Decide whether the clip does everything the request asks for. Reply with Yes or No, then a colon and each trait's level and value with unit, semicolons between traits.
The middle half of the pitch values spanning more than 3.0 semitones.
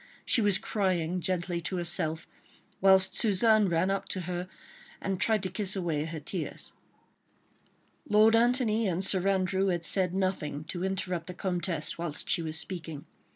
No: narrow, 2.4 semitones